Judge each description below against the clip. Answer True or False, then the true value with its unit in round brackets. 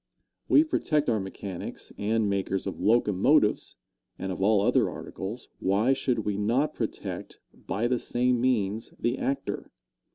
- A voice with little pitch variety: False (4.1 semitones)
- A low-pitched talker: True (110 Hz)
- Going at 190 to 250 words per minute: False (140 wpm)